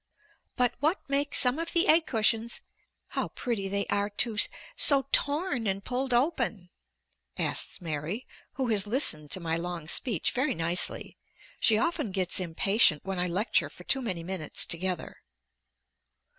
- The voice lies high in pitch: Yes, high, 215 Hz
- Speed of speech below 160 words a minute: Yes, average, 150 wpm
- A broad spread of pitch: Yes, wide, 6.5 semitones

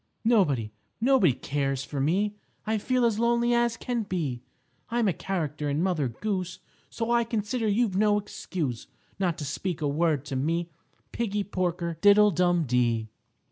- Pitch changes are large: Yes, wide, 6.6 semitones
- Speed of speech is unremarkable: Yes, average, 160 wpm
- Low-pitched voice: No, medium, 185 Hz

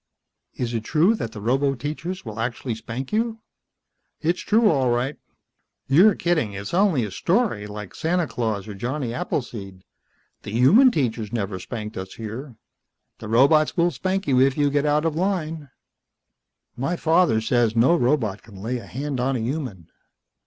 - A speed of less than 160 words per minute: No, average, 165 wpm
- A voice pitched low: Yes, low, 130 Hz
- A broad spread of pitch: Yes, wide, 6.3 semitones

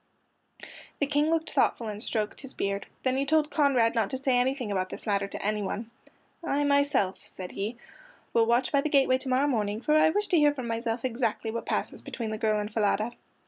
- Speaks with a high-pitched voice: Yes, high, 240 Hz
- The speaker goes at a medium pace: No, fast, 215 wpm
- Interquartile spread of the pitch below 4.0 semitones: No, average, 4.8 semitones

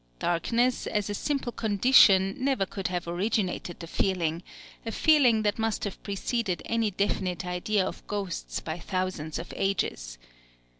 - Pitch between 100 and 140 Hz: No, high, 195 Hz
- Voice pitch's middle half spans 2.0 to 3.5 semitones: No, average, 4.0 semitones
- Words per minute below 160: Yes, average, 145 wpm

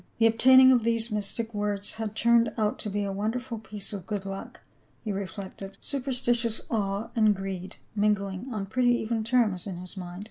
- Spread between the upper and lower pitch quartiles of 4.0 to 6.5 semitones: No, average, 3.0 semitones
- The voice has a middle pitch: No, high, 210 Hz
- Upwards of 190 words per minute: No, average, 180 wpm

